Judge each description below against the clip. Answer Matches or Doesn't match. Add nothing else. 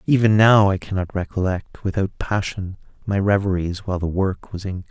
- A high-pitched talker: Doesn't match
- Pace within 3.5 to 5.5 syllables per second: Doesn't match